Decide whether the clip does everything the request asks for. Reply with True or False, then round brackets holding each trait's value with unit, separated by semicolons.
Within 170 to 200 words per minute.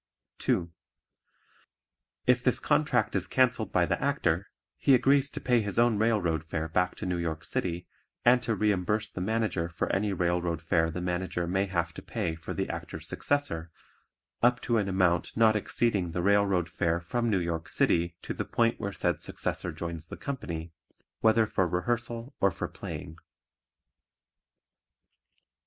False (160 wpm)